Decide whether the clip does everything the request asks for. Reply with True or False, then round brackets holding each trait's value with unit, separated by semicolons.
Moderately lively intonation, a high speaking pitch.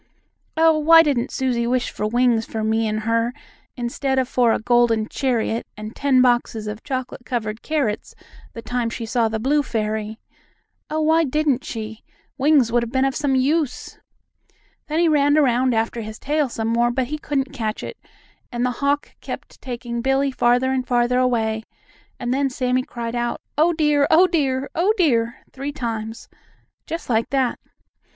True (3.5 semitones; 250 Hz)